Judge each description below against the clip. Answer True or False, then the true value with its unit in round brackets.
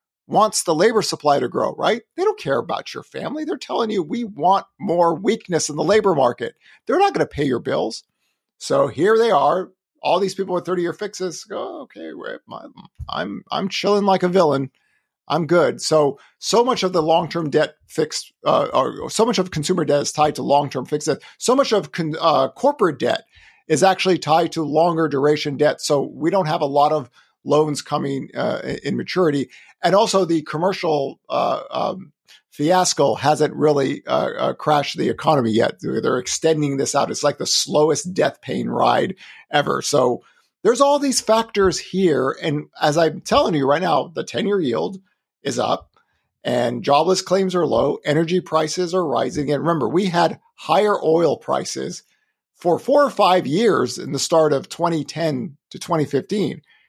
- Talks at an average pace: True (180 wpm)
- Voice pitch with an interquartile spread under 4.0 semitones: False (4.5 semitones)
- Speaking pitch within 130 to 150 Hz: False (170 Hz)